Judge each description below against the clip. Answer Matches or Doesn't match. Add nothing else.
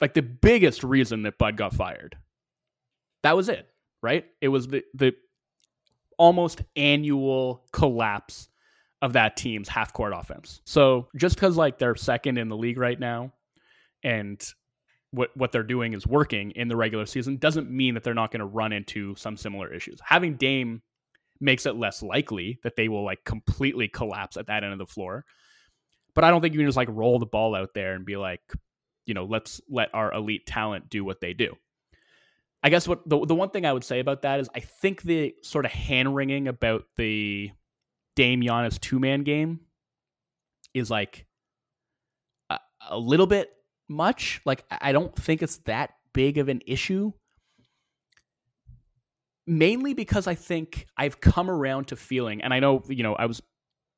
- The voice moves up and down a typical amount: Matches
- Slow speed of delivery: Doesn't match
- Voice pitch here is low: Matches